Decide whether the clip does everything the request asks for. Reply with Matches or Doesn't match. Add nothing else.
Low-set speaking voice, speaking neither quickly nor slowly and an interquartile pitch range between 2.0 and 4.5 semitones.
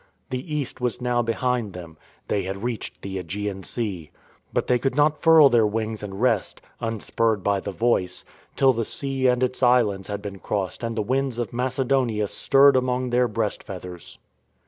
Matches